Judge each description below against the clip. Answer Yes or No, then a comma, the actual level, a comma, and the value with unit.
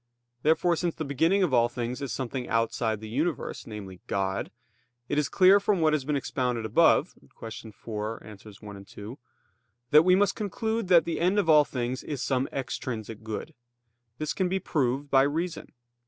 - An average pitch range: No, wide, 6.5 semitones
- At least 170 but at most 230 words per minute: Yes, average, 180 wpm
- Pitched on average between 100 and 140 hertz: Yes, low, 135 Hz